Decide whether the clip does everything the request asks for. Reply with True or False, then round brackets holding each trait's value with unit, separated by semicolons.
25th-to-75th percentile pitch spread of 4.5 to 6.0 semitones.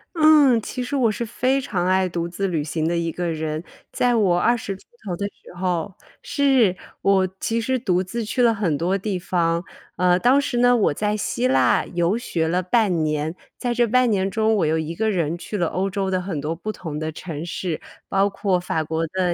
True (4.8 semitones)